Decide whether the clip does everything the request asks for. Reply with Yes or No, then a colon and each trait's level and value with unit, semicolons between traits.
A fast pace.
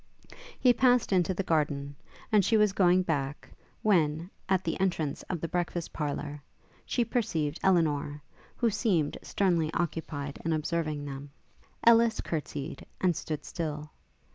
No: average, 140 wpm